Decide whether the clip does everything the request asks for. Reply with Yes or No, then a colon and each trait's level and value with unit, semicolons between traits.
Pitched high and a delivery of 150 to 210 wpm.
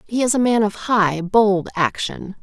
Yes: high, 205 Hz; average, 200 wpm